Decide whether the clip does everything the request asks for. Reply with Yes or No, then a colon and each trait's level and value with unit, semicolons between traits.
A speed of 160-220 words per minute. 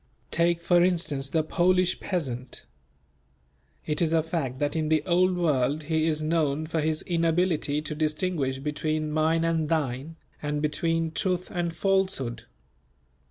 No: average, 145 wpm